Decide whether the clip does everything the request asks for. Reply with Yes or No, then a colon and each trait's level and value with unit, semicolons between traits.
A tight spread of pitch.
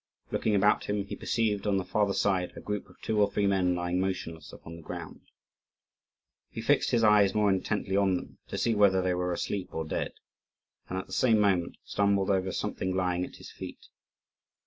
Yes: narrow, 2.2 semitones